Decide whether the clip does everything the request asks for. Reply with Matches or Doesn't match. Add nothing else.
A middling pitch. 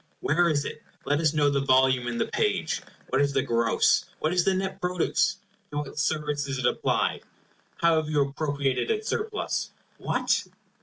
Matches